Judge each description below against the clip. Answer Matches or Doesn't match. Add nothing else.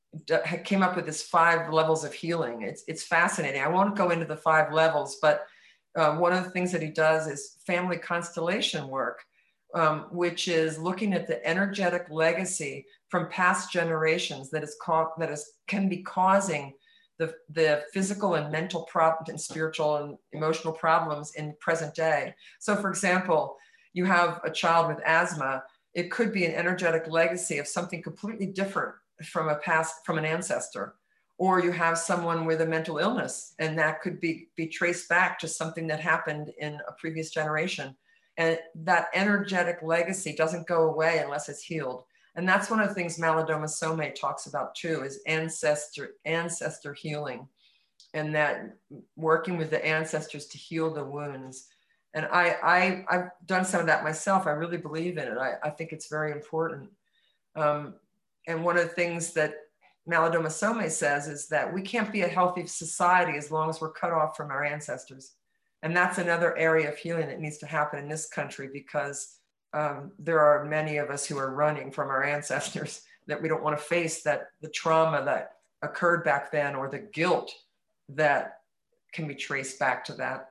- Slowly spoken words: Doesn't match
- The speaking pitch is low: Doesn't match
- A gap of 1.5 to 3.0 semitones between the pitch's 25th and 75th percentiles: Matches